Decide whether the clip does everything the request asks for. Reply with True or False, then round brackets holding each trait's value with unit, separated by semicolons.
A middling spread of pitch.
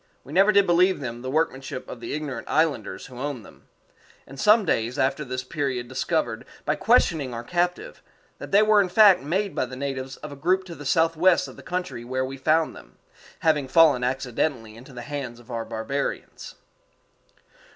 True (5.0 semitones)